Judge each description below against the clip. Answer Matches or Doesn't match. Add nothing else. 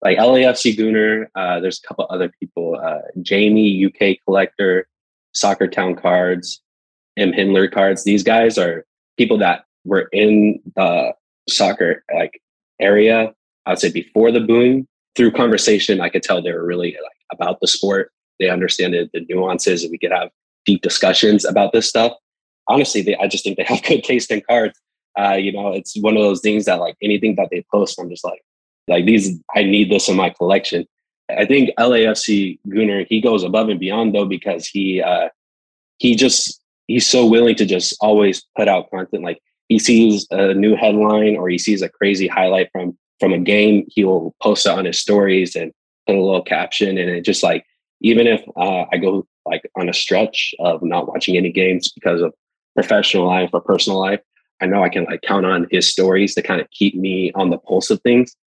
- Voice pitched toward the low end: Matches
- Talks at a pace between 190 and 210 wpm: Matches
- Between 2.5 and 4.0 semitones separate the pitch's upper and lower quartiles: Matches